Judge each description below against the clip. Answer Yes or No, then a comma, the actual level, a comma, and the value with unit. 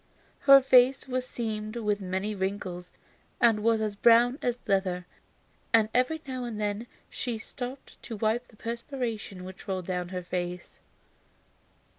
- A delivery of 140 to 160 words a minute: Yes, average, 145 wpm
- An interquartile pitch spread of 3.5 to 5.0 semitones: Yes, average, 4.2 semitones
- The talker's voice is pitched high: Yes, high, 220 Hz